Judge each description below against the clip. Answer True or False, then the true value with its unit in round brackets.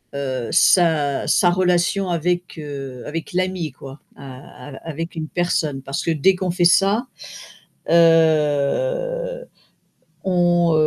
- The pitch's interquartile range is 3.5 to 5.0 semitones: True (4.1 semitones)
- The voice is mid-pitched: True (165 Hz)